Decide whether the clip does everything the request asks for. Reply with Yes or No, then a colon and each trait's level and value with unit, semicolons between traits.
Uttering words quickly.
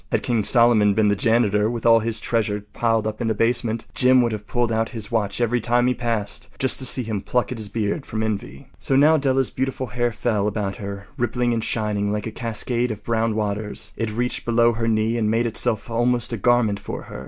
Yes: fast, 230 wpm